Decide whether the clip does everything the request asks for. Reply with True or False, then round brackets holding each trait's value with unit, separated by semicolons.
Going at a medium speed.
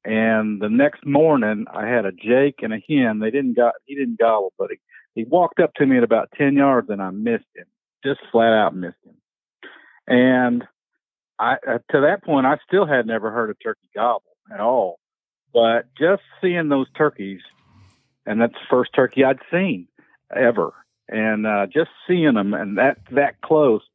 True (185 wpm)